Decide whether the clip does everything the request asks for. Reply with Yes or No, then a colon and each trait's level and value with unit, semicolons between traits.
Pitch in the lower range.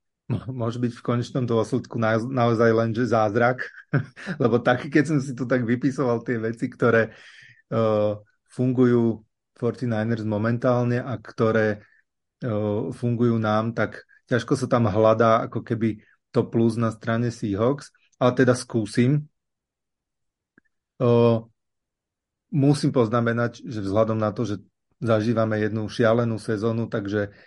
Yes: low, 115 Hz